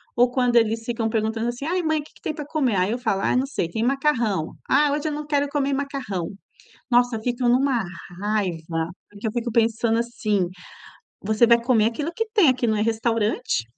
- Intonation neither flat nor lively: Yes, average, 4.0 semitones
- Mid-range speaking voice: No, high, 235 Hz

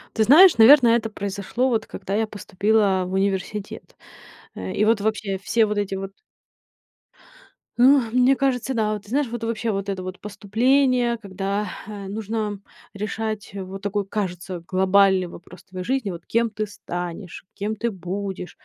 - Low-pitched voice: No, high, 205 Hz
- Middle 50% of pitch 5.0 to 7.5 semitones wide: No, average, 2.8 semitones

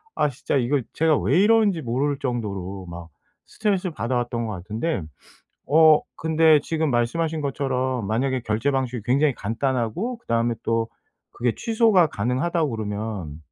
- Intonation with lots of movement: Yes, wide, 5.8 semitones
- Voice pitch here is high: No, low, 130 Hz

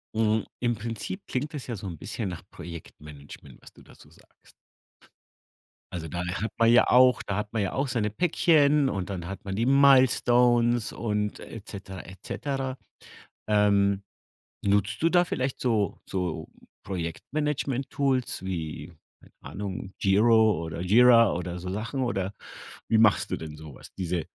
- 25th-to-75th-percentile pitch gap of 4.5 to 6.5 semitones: Yes, average, 5.0 semitones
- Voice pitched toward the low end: Yes, low, 105 Hz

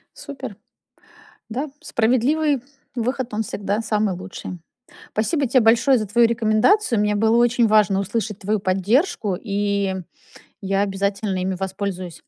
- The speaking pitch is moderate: No, high, 215 Hz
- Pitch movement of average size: Yes, average, 3.3 semitones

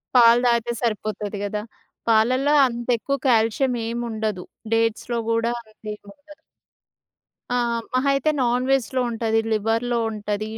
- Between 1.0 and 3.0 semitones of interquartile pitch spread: Yes, narrow, 2.4 semitones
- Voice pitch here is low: No, high, 230 Hz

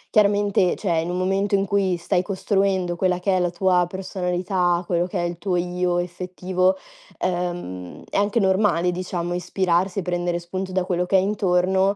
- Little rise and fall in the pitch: Yes, narrow, 1.5 semitones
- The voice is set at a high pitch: No, medium, 180 Hz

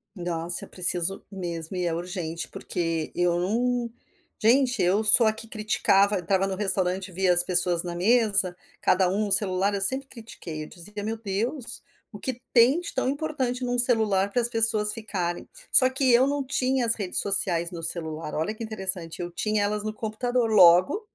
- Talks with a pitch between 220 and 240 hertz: No, high, 205 Hz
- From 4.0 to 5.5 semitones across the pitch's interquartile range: Yes, average, 4.7 semitones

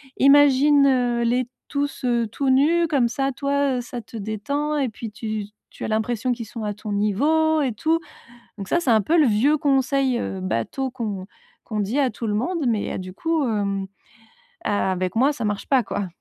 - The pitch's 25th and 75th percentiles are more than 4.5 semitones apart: Yes, average, 4.9 semitones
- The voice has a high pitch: Yes, high, 245 Hz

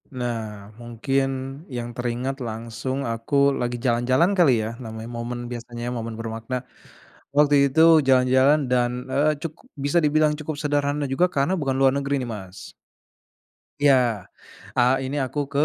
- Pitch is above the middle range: No, low, 130 Hz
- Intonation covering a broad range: No, average, 3.3 semitones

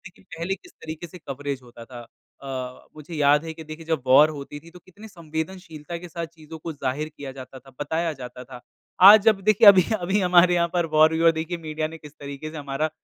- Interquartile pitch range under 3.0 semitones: No, average, 3.4 semitones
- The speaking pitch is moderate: Yes, medium, 160 Hz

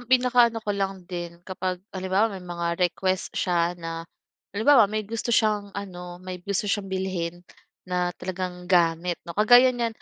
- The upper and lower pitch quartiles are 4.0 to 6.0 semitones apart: No, average, 3.0 semitones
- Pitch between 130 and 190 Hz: Yes, medium, 185 Hz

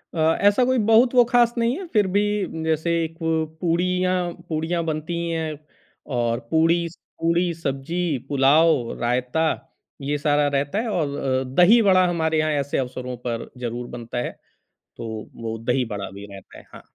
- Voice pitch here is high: No, medium, 160 Hz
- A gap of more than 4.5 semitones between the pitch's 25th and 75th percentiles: Yes, average, 5.2 semitones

